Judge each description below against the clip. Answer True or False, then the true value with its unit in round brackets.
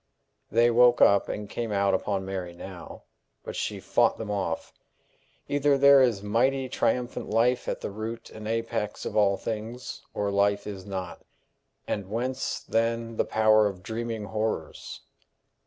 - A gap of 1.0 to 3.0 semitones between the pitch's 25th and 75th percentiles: True (2.7 semitones)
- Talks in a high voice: False (110 Hz)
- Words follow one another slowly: False (155 wpm)